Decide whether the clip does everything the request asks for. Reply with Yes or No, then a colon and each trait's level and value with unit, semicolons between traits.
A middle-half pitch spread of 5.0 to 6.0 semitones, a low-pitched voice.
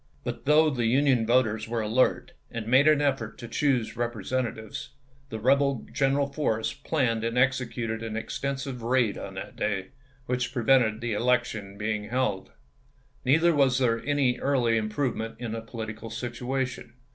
No: average, 3.1 semitones; low, 120 Hz